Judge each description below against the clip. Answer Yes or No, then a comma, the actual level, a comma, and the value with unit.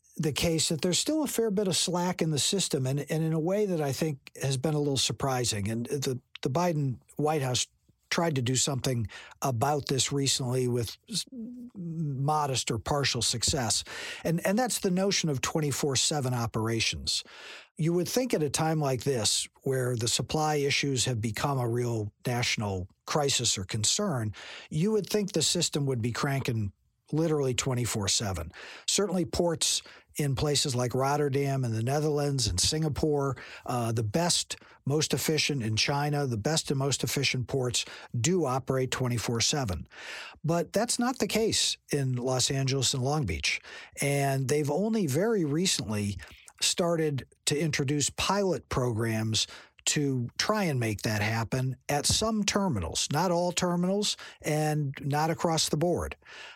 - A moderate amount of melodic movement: Yes, average, 4.8 semitones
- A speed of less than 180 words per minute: Yes, average, 155 wpm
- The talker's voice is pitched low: No, medium, 145 Hz